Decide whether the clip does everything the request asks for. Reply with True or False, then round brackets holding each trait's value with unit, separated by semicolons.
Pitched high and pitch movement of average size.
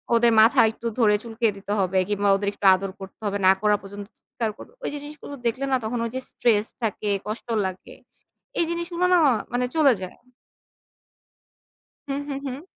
True (225 Hz; 4.8 semitones)